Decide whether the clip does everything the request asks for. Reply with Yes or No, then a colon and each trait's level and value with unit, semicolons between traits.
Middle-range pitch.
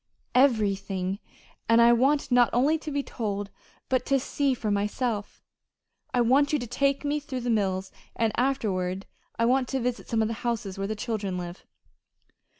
No: high, 235 Hz